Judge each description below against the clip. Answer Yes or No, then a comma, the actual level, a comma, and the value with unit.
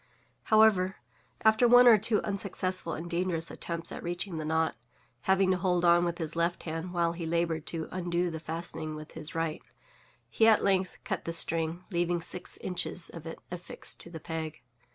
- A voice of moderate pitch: Yes, medium, 170 Hz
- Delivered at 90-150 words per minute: No, average, 185 wpm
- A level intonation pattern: Yes, narrow, 2.1 semitones